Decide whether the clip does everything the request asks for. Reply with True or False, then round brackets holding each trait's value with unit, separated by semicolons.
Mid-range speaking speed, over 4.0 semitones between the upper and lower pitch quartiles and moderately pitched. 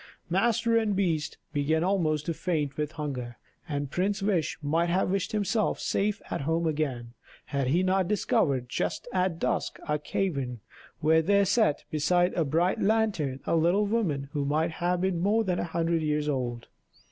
True (170 wpm; 4.5 semitones; 165 Hz)